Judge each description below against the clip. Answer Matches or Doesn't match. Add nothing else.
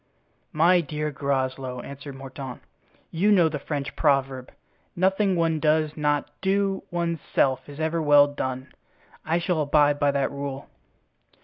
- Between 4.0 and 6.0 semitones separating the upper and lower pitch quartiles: Doesn't match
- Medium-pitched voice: Matches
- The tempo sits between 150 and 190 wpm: Doesn't match